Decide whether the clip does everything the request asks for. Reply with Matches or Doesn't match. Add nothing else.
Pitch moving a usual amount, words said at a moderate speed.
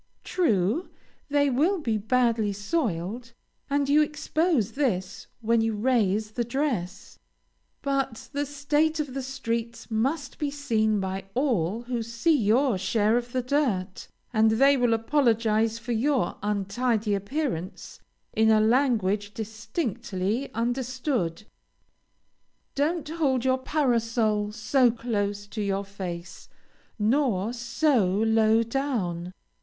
Doesn't match